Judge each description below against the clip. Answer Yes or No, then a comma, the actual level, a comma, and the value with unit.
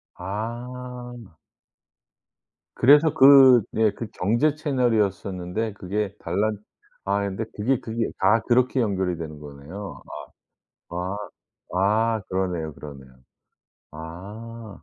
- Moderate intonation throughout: Yes, average, 4.6 semitones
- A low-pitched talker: Yes, low, 105 Hz